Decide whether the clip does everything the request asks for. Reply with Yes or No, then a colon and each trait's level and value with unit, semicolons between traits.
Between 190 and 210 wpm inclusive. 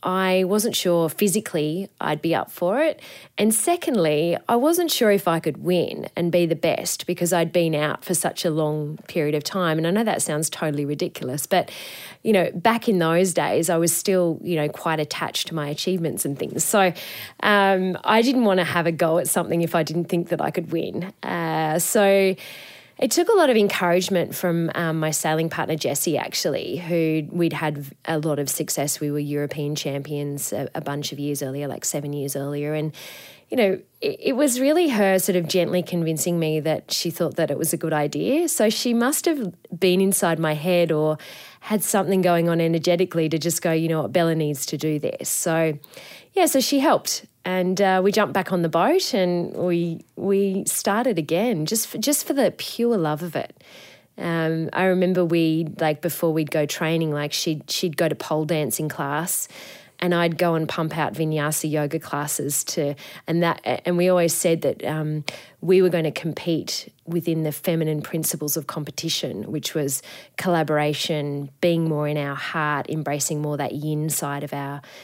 Yes: average, 200 wpm